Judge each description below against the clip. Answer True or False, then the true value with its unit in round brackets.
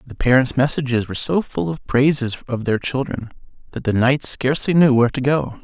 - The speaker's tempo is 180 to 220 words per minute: True (200 wpm)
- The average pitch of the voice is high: False (130 Hz)